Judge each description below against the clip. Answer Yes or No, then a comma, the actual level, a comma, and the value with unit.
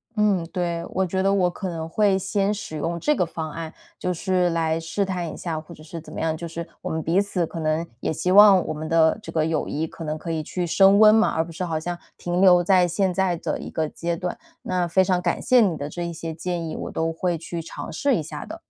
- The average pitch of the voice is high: No, medium, 170 Hz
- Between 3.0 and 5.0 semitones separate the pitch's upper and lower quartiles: No, narrow, 2.6 semitones